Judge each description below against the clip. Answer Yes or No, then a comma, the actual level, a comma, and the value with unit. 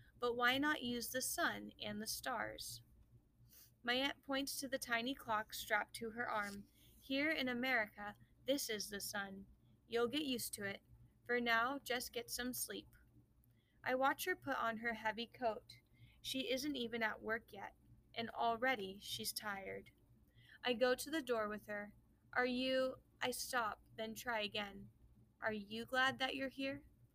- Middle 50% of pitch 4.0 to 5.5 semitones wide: Yes, average, 4.3 semitones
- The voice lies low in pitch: No, high, 230 Hz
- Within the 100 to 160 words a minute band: No, average, 170 wpm